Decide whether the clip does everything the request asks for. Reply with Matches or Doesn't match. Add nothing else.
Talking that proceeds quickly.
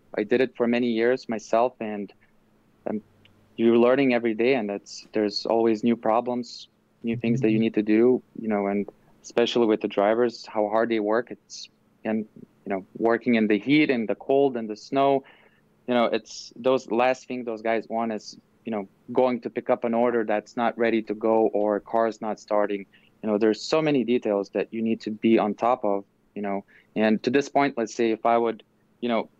Matches